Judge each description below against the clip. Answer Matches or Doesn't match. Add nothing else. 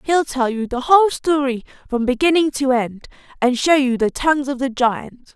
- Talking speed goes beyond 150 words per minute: Matches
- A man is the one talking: Doesn't match